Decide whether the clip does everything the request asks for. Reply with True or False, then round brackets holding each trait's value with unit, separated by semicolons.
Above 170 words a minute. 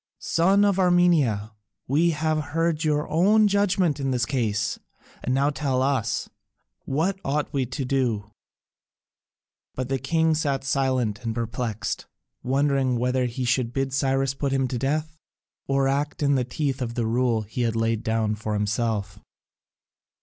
False (155 wpm)